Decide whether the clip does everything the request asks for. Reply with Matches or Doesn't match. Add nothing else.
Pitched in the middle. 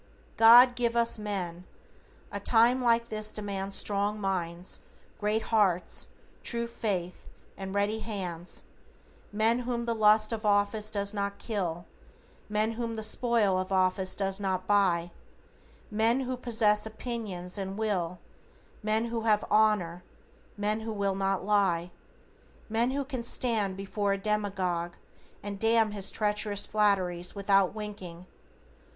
Doesn't match